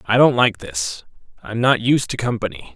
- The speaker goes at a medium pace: No, fast, 220 wpm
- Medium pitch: No, low, 115 Hz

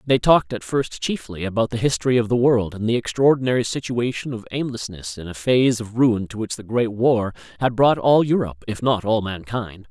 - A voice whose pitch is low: Yes, low, 115 Hz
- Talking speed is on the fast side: Yes, fast, 210 wpm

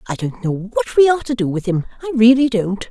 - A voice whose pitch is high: Yes, high, 220 Hz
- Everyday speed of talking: No, fast, 270 wpm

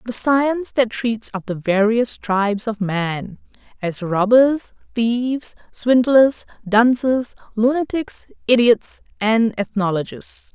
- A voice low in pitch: No, high, 225 Hz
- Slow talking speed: Yes, slow, 110 wpm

